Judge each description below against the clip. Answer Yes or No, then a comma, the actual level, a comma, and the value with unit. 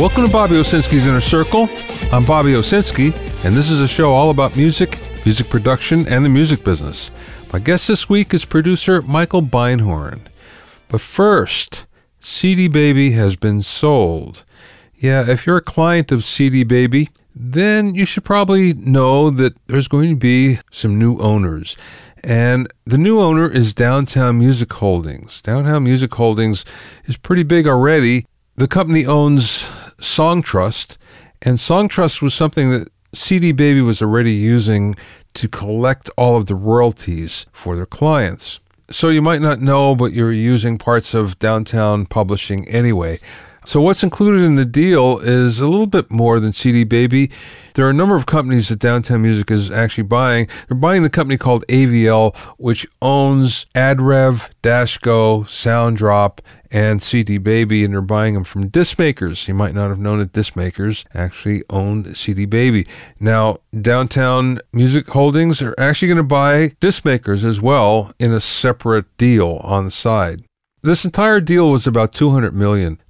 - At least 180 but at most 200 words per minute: No, average, 160 wpm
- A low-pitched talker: Yes, low, 125 Hz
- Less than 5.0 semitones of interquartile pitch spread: No, wide, 5.6 semitones